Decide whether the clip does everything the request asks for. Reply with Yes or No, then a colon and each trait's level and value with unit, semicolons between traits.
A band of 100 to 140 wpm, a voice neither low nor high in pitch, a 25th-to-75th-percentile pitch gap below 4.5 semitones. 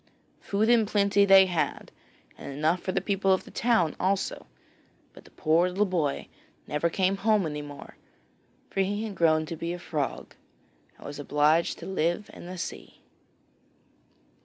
No: average, 165 wpm; medium, 180 Hz; average, 4.0 semitones